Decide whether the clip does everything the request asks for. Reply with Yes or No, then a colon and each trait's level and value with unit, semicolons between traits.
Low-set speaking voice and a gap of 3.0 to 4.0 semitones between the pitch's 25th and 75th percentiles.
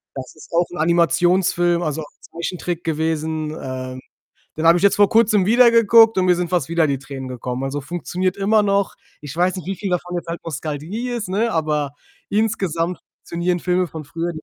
No: medium, 175 Hz; average, 3.5 semitones